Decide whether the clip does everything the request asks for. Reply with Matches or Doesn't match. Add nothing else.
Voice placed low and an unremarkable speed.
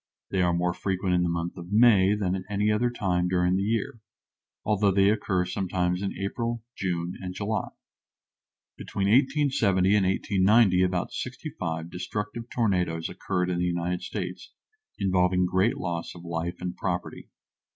Matches